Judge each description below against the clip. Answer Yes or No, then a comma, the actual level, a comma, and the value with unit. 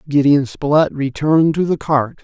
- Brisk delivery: No, average, 160 wpm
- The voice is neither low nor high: Yes, medium, 145 Hz